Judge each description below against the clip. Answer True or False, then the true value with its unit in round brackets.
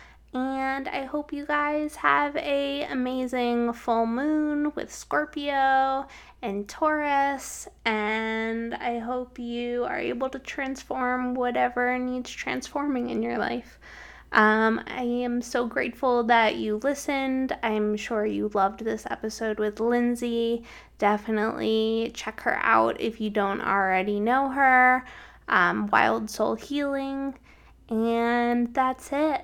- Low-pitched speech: False (245 Hz)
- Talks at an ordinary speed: False (125 wpm)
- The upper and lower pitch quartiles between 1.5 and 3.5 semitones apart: True (3.2 semitones)